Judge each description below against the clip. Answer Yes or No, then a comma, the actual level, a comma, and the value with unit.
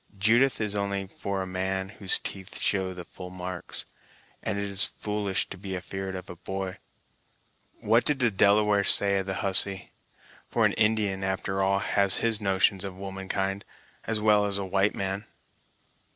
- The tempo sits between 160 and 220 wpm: Yes, average, 170 wpm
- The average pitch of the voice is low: Yes, very low, 95 Hz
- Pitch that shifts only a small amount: Yes, narrow, 1.3 semitones